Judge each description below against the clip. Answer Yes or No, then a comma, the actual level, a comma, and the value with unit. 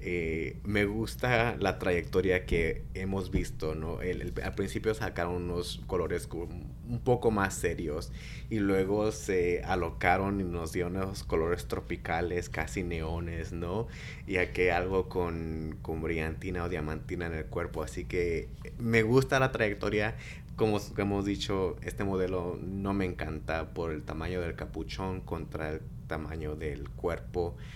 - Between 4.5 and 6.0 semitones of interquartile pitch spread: No, average, 3.4 semitones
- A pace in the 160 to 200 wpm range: No, average, 145 wpm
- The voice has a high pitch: No, very low, 90 Hz